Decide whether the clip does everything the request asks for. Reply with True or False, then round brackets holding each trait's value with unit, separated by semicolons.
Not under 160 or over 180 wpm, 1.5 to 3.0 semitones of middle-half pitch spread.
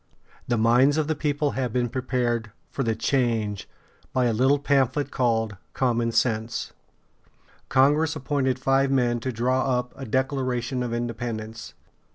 False (150 wpm; 2.5 semitones)